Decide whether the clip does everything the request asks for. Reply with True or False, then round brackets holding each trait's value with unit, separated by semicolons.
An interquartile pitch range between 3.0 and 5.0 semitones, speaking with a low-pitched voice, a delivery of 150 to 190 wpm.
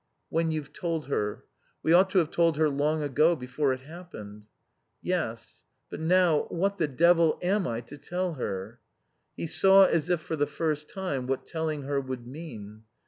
False (4.4 semitones; 155 Hz; 180 wpm)